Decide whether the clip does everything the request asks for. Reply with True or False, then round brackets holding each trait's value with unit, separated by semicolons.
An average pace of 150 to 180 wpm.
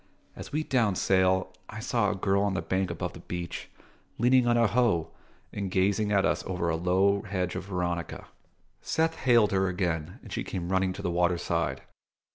False (190 wpm)